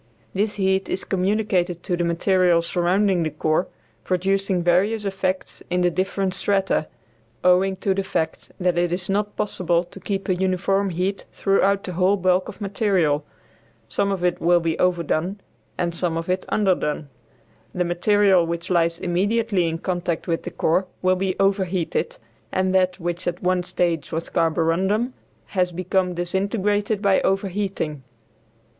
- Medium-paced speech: Yes, average, 155 wpm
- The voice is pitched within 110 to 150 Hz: No, medium, 185 Hz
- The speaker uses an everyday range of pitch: No, narrow, 2.0 semitones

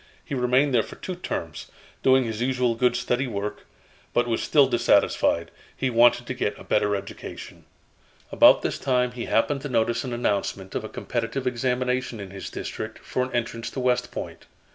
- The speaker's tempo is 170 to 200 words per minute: Yes, average, 185 wpm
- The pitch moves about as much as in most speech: No, narrow, 2.0 semitones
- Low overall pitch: Yes, low, 120 Hz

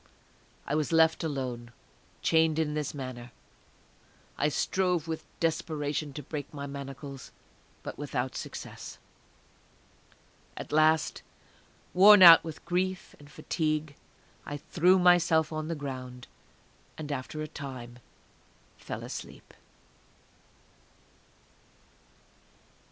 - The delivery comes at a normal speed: No, slow, 100 wpm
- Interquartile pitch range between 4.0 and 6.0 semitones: No, average, 2.7 semitones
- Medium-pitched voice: Yes, medium, 150 Hz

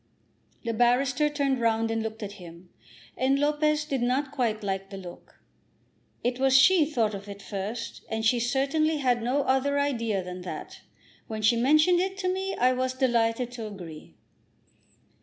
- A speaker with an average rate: Yes, average, 170 wpm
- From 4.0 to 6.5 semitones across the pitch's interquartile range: Yes, average, 4.5 semitones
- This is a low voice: No, high, 245 Hz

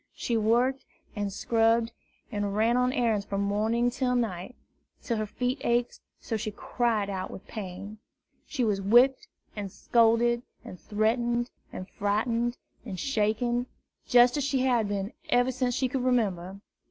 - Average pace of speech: Yes, average, 155 wpm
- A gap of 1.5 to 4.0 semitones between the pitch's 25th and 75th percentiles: Yes, average, 3.0 semitones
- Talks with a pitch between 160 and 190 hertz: No, high, 230 Hz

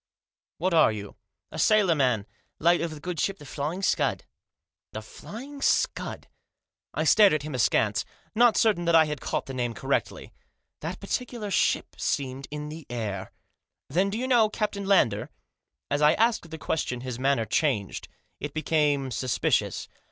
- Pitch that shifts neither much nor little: No, wide, 7.1 semitones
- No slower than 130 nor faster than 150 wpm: No, average, 175 wpm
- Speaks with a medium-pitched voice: Yes, medium, 155 Hz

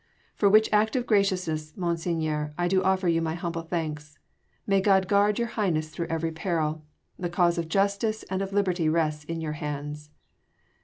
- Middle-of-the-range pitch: Yes, medium, 170 Hz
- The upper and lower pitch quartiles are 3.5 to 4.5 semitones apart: Yes, average, 3.8 semitones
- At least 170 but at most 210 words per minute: Yes, average, 175 wpm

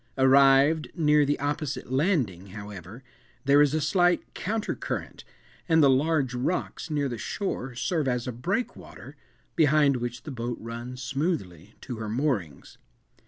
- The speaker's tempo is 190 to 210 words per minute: No, average, 145 wpm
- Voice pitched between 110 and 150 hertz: Yes, low, 135 Hz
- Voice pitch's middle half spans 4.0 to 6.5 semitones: Yes, average, 4.3 semitones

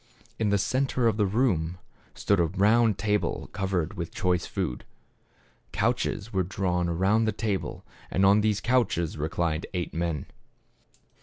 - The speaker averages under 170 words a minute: Yes, average, 145 wpm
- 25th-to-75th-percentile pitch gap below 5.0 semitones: Yes, average, 3.7 semitones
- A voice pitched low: Yes, very low, 95 Hz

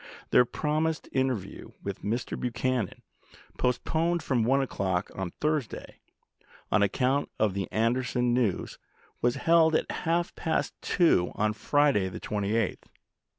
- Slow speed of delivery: Yes, slow, 125 wpm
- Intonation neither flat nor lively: No, wide, 5.7 semitones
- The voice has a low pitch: Yes, low, 125 Hz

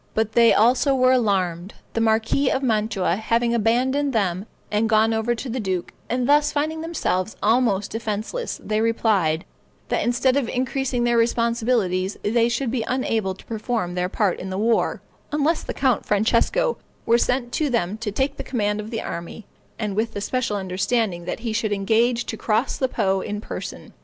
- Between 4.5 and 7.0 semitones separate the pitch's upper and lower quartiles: No, average, 3.3 semitones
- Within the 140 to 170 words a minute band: No, average, 180 wpm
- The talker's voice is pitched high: Yes, high, 225 Hz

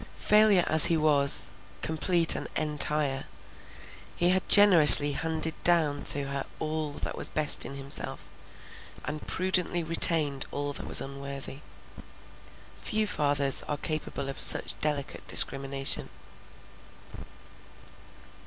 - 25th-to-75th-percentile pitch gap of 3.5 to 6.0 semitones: No, average, 2.9 semitones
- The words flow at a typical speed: No, slow, 115 wpm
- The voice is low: No, medium, 150 Hz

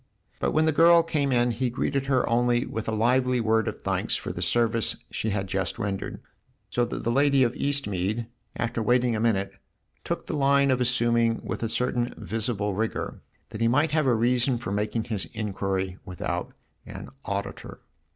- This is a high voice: No, low, 120 Hz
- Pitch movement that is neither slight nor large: Yes, average, 3.0 semitones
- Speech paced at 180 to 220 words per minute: Yes, average, 185 wpm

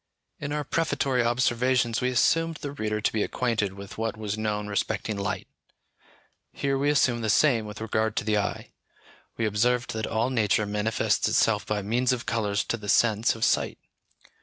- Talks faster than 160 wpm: Yes, average, 180 wpm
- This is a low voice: Yes, low, 110 Hz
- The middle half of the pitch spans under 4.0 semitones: Yes, average, 3.0 semitones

